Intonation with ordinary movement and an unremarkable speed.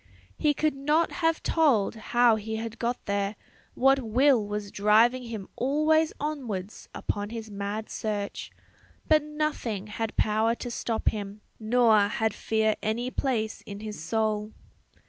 Yes: average, 3.8 semitones; average, 145 wpm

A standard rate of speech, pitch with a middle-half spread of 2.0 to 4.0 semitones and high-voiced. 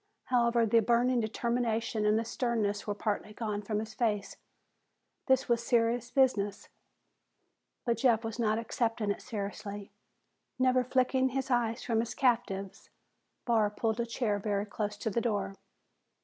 Yes: average, 150 wpm; narrow, 2.4 semitones; high, 230 Hz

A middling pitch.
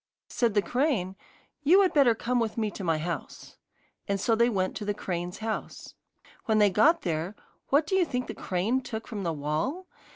No: high, 220 Hz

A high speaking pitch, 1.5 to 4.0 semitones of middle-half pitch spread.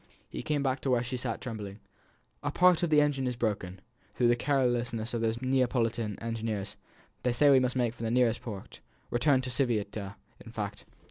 No: low, 120 Hz; average, 2.7 semitones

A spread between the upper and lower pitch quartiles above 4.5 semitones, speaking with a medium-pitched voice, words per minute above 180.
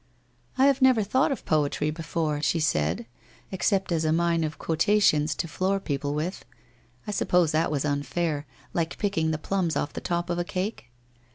No: average, 3.8 semitones; medium, 165 Hz; average, 200 wpm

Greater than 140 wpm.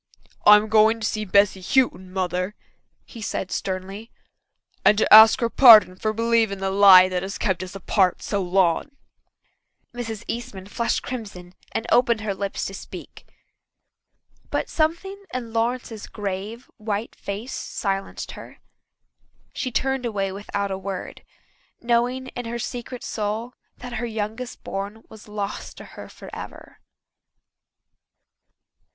No: slow, 135 wpm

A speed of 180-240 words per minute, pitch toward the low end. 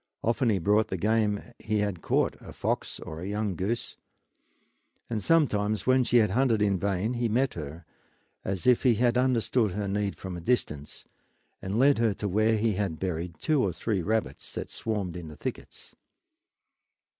Yes: average, 190 wpm; low, 105 Hz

